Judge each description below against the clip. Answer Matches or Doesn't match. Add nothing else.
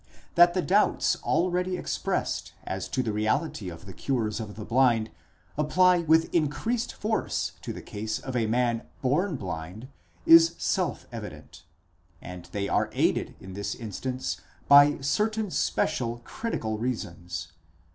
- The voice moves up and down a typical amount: Doesn't match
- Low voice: Matches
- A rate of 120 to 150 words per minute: Matches